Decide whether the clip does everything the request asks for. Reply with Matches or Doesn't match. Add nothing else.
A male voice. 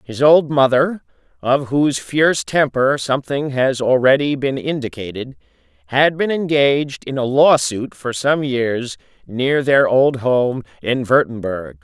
Matches